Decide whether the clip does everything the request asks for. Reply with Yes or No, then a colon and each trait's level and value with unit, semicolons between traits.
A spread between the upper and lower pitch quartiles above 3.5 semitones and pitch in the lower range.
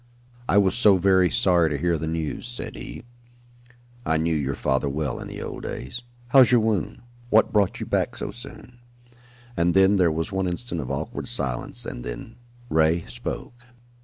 Yes: average, 4.7 semitones; very low, 90 Hz